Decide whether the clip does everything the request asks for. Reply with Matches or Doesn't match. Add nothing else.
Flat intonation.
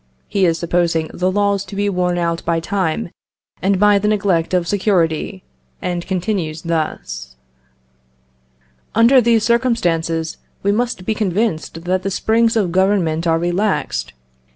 Doesn't match